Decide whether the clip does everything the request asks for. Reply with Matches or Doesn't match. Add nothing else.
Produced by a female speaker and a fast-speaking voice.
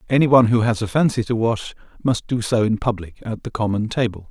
Doesn't match